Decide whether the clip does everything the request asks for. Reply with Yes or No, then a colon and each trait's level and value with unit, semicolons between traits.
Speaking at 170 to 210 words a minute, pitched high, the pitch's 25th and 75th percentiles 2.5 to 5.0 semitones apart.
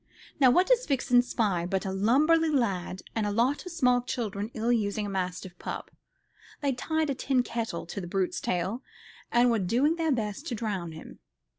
No: average, 190 wpm; high, 230 Hz; wide, 5.6 semitones